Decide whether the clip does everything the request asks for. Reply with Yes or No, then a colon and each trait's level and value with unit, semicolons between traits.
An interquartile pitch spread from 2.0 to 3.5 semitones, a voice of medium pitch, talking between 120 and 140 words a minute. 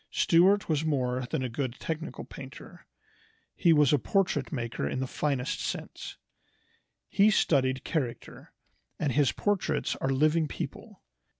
No: average, 3.9 semitones; medium, 145 Hz; slow, 135 wpm